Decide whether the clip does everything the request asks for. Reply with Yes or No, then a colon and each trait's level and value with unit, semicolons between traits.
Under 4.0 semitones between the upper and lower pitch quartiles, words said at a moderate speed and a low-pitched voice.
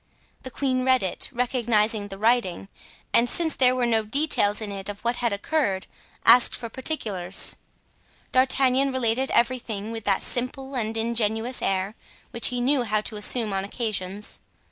No: average, 3.6 semitones; average, 160 wpm; high, 230 Hz